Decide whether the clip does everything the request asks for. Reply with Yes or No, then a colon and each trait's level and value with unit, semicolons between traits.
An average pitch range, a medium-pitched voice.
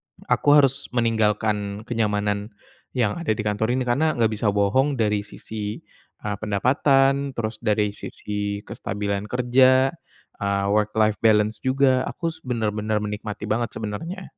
No: average, 3.6 semitones; low, 110 Hz